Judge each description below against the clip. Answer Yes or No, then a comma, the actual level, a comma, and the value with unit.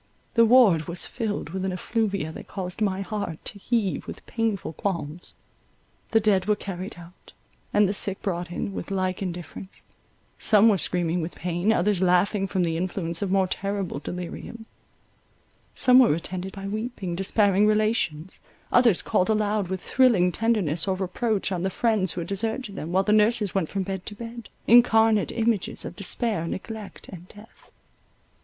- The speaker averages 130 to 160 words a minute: No, average, 170 wpm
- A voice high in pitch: Yes, high, 195 Hz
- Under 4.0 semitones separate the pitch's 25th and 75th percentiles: Yes, average, 3.3 semitones